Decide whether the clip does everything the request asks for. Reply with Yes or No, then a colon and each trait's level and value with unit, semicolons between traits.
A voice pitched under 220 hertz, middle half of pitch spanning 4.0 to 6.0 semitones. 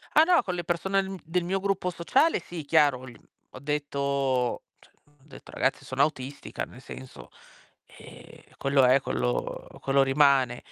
Yes: medium, 140 Hz; average, 4.8 semitones